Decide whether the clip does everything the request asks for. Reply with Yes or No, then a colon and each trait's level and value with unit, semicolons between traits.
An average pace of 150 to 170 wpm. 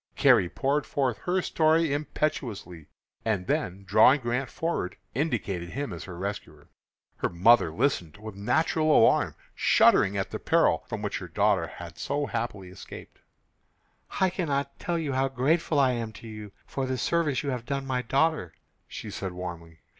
Yes: average, 160 wpm